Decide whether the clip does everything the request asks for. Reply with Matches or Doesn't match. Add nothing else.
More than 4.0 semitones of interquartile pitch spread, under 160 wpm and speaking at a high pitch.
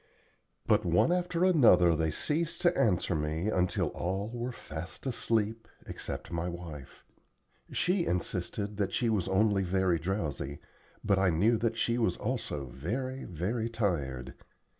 Doesn't match